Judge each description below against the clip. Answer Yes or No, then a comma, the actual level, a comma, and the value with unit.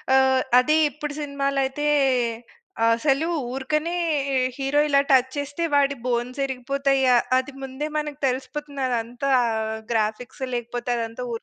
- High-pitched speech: Yes, very high, 270 Hz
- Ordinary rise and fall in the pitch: No, narrow, 2.2 semitones